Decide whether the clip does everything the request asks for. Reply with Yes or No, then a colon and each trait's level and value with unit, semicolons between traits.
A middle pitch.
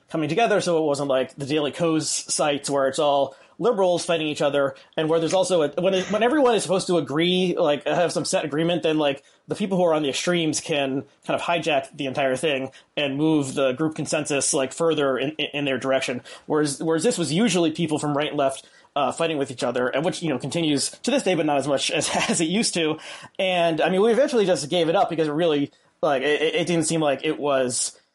Yes: medium, 155 Hz